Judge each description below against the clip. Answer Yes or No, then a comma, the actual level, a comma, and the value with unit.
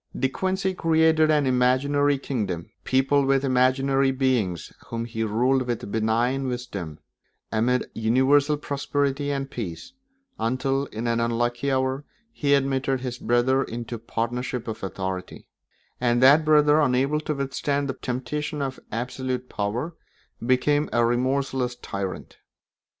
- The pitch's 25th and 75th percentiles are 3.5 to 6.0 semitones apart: No, average, 2.9 semitones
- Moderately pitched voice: No, low, 130 Hz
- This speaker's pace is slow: Yes, slow, 130 wpm